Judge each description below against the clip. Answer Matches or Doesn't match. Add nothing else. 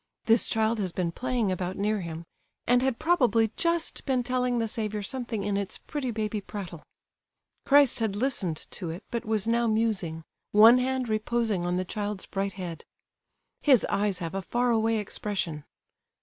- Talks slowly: Doesn't match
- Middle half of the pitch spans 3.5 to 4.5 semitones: Matches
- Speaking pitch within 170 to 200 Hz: Doesn't match